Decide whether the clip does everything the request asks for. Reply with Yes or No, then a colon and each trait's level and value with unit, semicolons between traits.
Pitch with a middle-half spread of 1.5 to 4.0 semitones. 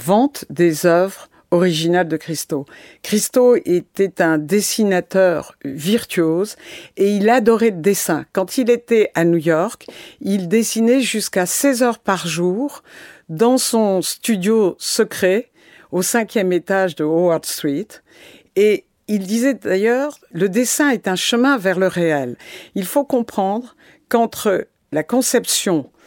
No: average, 5.0 semitones